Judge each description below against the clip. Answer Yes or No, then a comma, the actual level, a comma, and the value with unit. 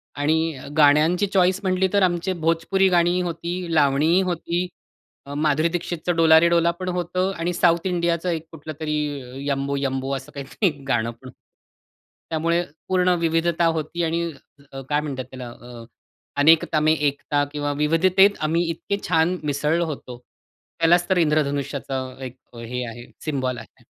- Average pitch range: Yes, average, 3.4 semitones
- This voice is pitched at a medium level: Yes, medium, 160 Hz